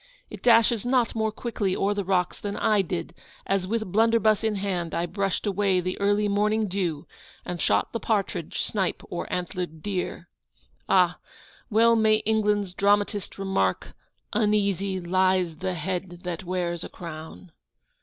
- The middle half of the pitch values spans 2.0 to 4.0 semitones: Yes, average, 2.9 semitones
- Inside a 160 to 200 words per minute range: No, average, 150 wpm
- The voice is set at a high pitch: Yes, high, 195 Hz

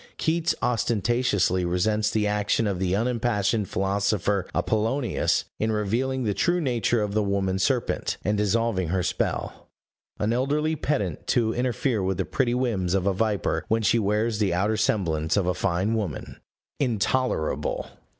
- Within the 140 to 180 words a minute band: Yes, average, 150 wpm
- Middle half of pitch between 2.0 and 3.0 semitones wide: No, average, 3.7 semitones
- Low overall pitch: Yes, low, 105 Hz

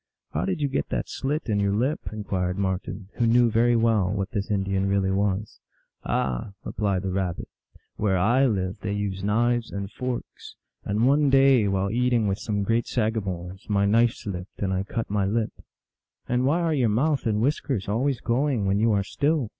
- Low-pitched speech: Yes, low, 105 Hz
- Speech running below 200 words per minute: No, fast, 205 wpm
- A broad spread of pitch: No, average, 3.6 semitones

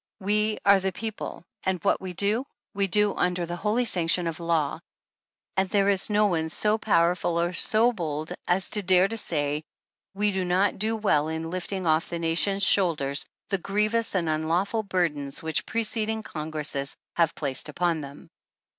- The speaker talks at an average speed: Yes, average, 175 wpm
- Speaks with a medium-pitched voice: Yes, medium, 180 Hz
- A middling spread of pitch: Yes, average, 4.1 semitones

